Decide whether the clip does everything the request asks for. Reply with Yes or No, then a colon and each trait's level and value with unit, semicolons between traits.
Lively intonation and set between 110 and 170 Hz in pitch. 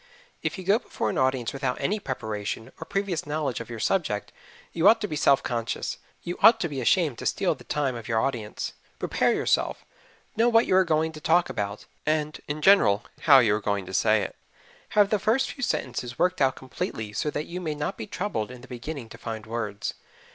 Yes: wide, 7.3 semitones; medium, 140 Hz